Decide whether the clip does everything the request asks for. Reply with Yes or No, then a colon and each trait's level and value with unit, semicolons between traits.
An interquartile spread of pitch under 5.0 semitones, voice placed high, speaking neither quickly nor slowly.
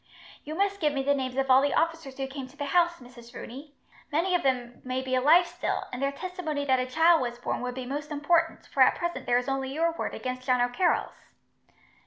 No: average, 4.3 semitones; very high, 275 Hz; fast, 235 wpm